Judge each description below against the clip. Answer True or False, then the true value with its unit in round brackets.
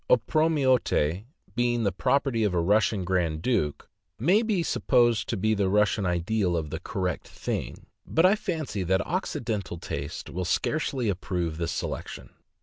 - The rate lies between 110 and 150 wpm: True (145 wpm)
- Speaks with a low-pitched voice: True (105 Hz)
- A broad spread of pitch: True (6.4 semitones)